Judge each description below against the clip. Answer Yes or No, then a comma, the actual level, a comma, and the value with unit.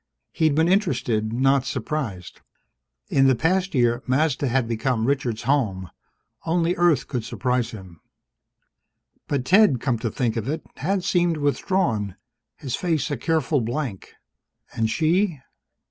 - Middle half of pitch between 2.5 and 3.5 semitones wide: No, wide, 5.5 semitones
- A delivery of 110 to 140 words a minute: Yes, slow, 135 wpm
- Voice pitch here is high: No, low, 135 Hz